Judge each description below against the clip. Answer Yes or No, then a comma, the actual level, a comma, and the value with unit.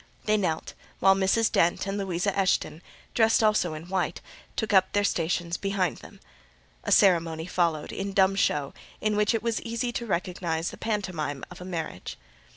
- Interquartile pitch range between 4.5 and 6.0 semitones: No, average, 3.5 semitones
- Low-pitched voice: No, high, 190 Hz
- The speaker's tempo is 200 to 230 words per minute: No, average, 170 wpm